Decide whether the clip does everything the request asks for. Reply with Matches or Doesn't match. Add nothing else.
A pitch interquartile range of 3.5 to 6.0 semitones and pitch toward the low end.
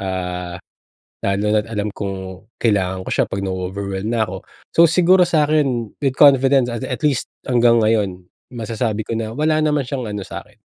Matches